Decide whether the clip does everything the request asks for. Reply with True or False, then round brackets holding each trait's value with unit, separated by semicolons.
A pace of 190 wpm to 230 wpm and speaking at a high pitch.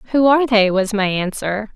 True (205 wpm; 215 Hz)